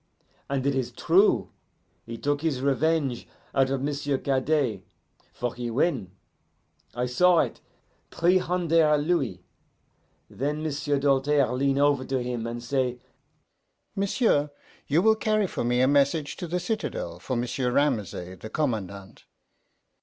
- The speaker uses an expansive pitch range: No, average, 4.1 semitones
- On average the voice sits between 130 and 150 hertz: Yes, medium, 140 Hz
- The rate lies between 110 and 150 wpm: Yes, average, 140 wpm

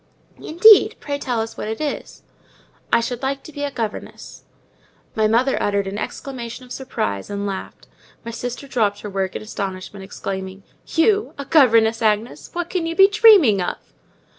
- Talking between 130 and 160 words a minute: No, average, 170 wpm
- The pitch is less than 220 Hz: No, high, 235 Hz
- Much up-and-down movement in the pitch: Yes, wide, 5.7 semitones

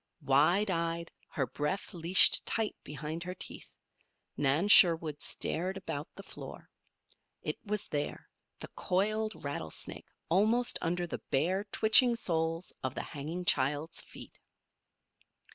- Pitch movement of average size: Yes, average, 4.8 semitones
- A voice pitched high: No, medium, 170 Hz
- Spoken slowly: Yes, slow, 125 wpm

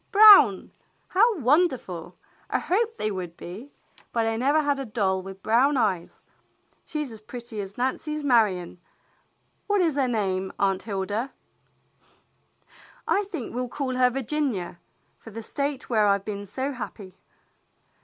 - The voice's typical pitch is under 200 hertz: No, high, 235 Hz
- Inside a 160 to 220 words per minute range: No, average, 145 wpm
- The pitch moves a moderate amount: No, wide, 6.3 semitones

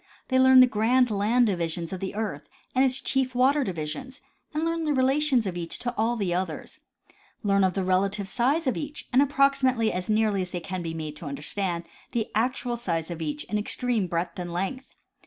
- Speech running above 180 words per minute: Yes, fast, 205 wpm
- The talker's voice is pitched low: No, high, 215 Hz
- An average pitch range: No, wide, 6.3 semitones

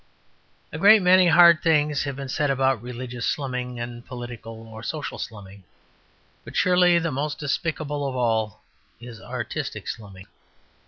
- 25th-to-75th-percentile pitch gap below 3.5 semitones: No, average, 4.7 semitones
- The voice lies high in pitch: No, low, 130 Hz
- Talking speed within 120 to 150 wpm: Yes, average, 145 wpm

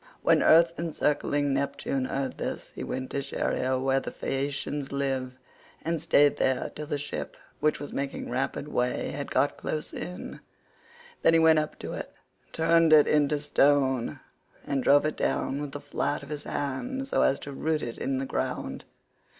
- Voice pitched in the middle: Yes, medium, 145 Hz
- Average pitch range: No, narrow, 2.1 semitones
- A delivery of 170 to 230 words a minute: Yes, average, 175 wpm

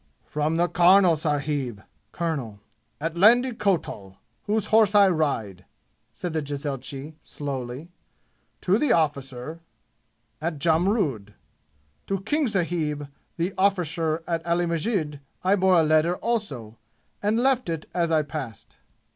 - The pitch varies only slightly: No, average, 4.6 semitones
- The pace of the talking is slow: Yes, slow, 125 wpm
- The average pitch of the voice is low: No, medium, 165 Hz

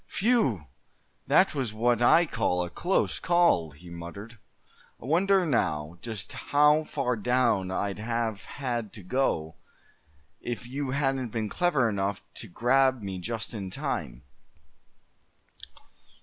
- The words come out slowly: Yes, slow, 130 wpm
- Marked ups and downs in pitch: Yes, wide, 5.8 semitones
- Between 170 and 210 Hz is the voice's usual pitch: No, low, 115 Hz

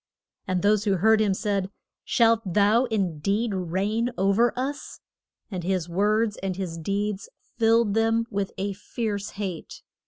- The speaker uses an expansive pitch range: No, average, 2.7 semitones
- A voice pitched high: Yes, high, 205 Hz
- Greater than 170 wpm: No, average, 150 wpm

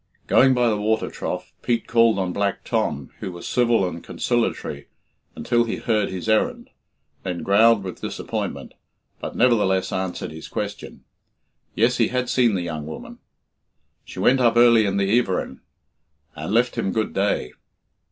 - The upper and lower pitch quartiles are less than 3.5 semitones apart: No, average, 3.8 semitones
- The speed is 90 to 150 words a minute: No, average, 160 wpm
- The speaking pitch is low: Yes, low, 110 Hz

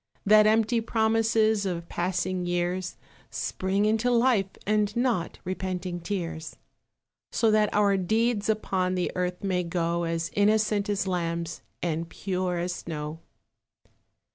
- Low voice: No, medium, 185 Hz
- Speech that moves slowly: Yes, slow, 125 wpm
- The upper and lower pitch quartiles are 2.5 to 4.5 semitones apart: Yes, average, 3.5 semitones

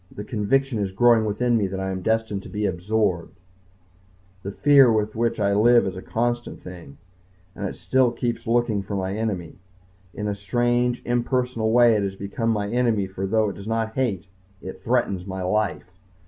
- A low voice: Yes, low, 110 Hz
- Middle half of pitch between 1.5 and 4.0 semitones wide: Yes, average, 3.5 semitones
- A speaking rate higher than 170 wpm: Yes, average, 190 wpm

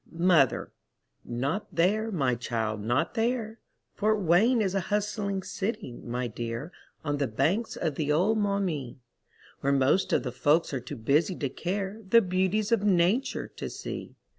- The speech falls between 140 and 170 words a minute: Yes, average, 160 wpm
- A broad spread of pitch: Yes, wide, 7.2 semitones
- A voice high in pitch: No, medium, 175 Hz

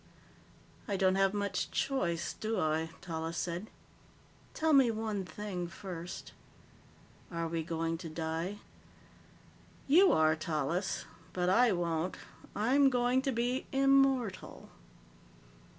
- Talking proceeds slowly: Yes, slow, 115 wpm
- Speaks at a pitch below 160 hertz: No, high, 190 Hz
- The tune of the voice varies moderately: No, wide, 6.5 semitones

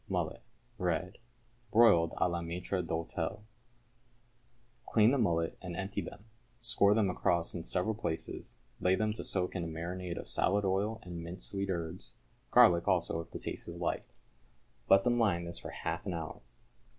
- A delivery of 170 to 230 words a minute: Yes, average, 175 wpm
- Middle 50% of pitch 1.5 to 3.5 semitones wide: Yes, average, 3.1 semitones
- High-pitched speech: No, very low, 90 Hz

